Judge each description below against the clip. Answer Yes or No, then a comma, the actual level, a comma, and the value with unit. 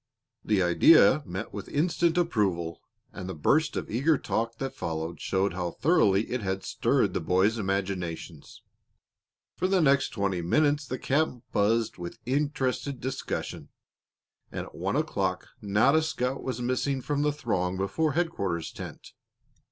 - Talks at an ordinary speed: Yes, average, 150 wpm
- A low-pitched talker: Yes, low, 115 Hz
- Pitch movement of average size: No, wide, 7.3 semitones